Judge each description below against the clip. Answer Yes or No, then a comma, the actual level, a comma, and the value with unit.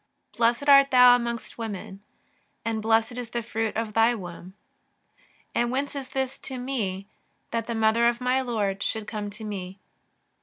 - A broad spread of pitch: No, average, 2.7 semitones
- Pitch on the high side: Yes, high, 230 Hz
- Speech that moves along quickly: No, average, 180 wpm